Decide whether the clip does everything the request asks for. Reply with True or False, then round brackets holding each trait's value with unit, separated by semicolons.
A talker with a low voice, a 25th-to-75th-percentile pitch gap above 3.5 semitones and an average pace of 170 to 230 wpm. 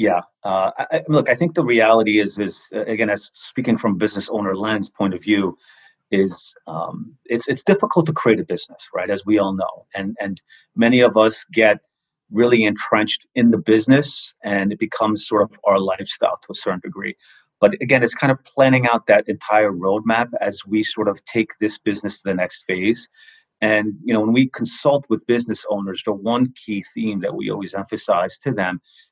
False (110 Hz; 3.1 semitones; 200 wpm)